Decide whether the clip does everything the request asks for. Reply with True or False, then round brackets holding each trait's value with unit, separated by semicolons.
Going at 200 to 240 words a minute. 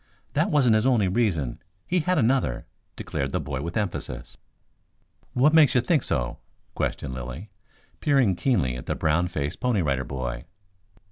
False (155 wpm)